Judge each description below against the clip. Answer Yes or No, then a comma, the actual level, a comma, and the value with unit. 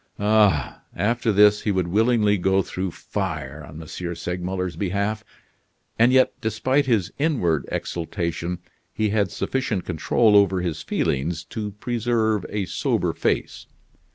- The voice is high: No, low, 100 Hz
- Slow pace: Yes, slow, 130 wpm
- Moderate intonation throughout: Yes, average, 3.8 semitones